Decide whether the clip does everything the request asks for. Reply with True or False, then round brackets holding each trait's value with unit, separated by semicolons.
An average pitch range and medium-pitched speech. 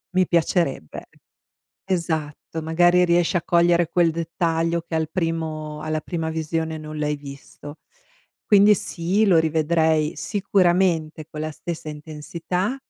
False (2.0 semitones; 165 Hz)